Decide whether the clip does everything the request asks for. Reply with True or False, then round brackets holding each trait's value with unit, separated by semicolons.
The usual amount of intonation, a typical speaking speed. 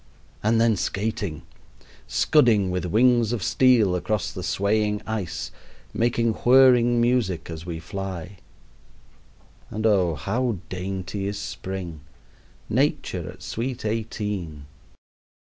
False (3.9 semitones; 110 wpm)